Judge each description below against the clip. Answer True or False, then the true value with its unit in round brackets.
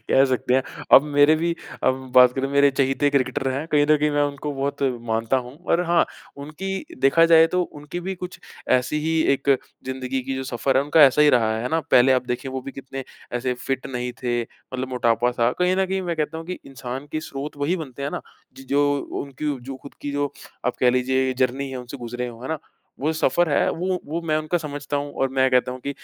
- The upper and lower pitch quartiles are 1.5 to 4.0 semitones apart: True (2.8 semitones)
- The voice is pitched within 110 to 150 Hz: True (140 Hz)